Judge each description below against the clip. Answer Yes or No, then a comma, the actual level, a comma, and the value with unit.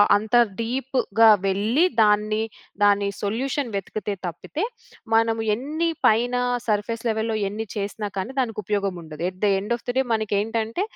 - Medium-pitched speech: No, high, 220 Hz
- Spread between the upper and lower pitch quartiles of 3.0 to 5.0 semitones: No, narrow, 2.4 semitones